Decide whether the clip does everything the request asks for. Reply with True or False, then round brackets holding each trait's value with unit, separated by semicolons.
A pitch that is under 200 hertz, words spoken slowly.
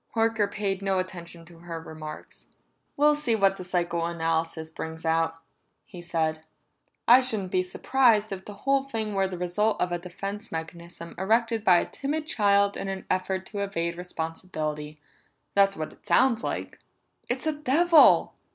False (190 Hz; 160 wpm)